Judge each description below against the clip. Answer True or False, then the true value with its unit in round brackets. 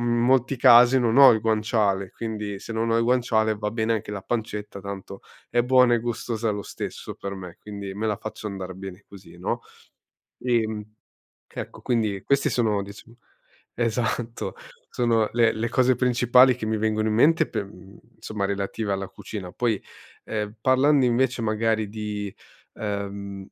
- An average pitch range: True (3.0 semitones)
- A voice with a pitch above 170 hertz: False (110 Hz)